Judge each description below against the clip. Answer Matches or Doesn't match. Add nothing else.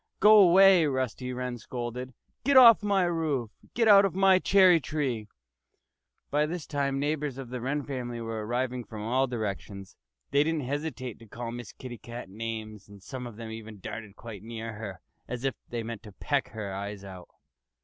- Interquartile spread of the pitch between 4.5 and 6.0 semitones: Matches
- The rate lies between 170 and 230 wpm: Matches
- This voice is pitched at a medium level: Doesn't match